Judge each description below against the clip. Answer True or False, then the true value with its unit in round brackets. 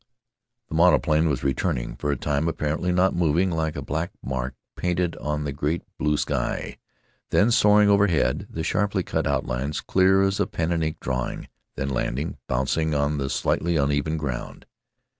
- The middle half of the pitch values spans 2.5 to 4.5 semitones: True (3.6 semitones)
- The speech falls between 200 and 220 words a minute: False (165 wpm)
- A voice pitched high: False (80 Hz)